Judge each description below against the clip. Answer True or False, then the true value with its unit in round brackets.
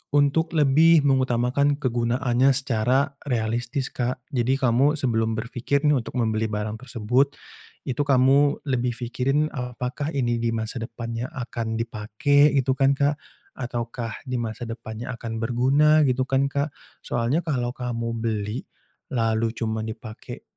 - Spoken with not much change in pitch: False (3.2 semitones)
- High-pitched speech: False (125 Hz)